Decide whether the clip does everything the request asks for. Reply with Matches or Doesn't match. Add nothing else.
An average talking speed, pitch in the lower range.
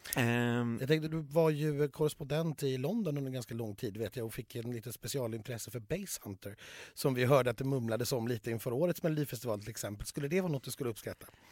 Doesn't match